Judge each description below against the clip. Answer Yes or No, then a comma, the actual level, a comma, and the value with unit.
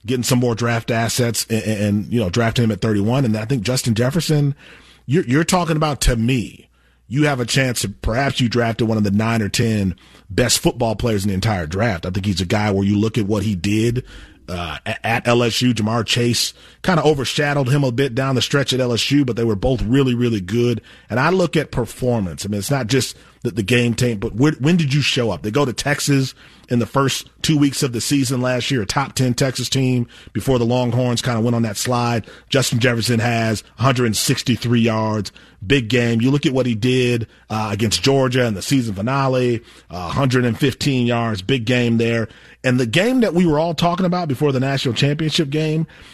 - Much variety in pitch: No, average, 3.4 semitones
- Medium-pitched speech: No, low, 120 Hz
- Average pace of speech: No, fast, 215 wpm